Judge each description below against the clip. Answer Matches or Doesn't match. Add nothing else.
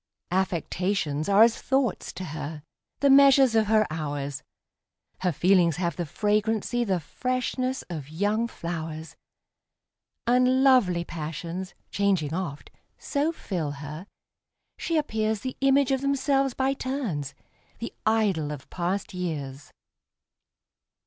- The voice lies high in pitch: Matches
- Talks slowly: Matches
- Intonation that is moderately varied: Doesn't match